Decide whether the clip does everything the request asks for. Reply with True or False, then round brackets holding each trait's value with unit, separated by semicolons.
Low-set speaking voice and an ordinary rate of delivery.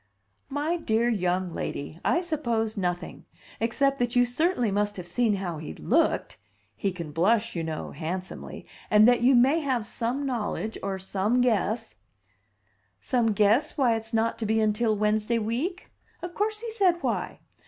False (225 Hz; 165 wpm)